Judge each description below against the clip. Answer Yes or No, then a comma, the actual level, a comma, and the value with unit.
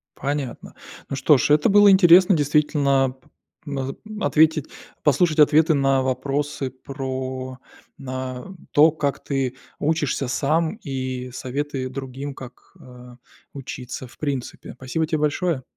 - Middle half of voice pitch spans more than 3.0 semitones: No, narrow, 2.6 semitones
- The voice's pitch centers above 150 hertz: No, medium, 140 Hz